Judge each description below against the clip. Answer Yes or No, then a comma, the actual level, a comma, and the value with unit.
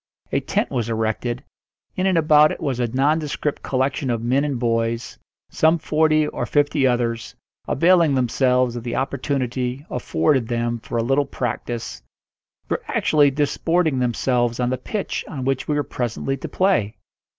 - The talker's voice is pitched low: Yes, low, 130 Hz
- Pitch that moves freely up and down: No, average, 3.8 semitones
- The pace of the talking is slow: No, average, 160 wpm